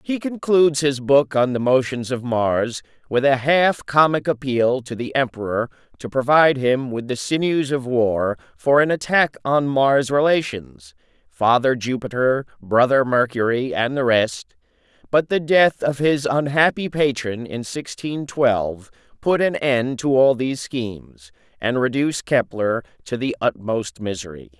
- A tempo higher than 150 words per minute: No, average, 145 wpm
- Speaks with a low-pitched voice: Yes, low, 130 Hz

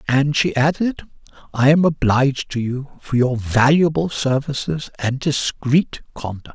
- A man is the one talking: Yes, male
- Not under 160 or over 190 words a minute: No, average, 140 wpm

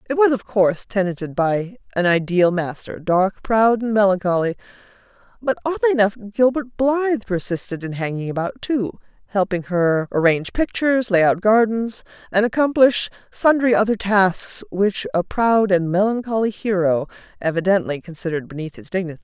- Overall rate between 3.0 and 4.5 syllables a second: No, 5.2 syllables/s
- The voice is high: Yes, high, 200 Hz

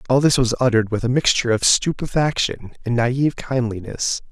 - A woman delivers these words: No, male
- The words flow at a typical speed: Yes, average, 165 wpm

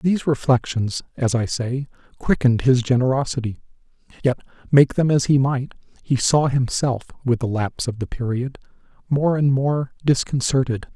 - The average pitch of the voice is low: Yes, low, 130 Hz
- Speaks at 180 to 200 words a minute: No, average, 150 wpm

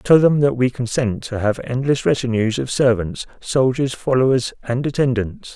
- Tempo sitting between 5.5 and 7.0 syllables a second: No, 4.8 syllables/s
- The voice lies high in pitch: No, low, 130 Hz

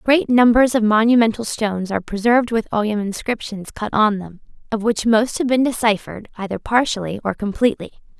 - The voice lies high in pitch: Yes, high, 220 Hz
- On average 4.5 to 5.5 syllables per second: No, 5.8 syllables/s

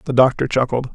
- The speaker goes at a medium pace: Yes, average, 190 wpm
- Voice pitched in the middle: No, low, 130 Hz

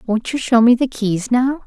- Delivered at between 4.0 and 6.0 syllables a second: Yes, 4.7 syllables/s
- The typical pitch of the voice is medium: No, high, 240 Hz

